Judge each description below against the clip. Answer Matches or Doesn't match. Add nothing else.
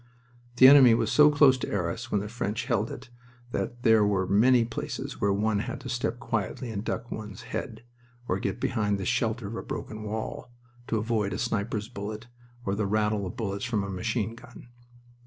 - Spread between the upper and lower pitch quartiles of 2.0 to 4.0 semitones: Matches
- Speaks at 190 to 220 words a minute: Matches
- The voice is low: Matches